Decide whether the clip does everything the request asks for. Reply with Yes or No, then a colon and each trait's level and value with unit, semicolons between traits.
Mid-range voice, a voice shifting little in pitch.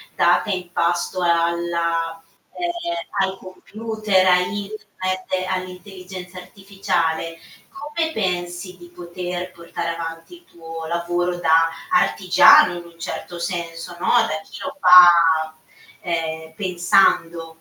Yes: medium, 175 Hz; narrow, 1.8 semitones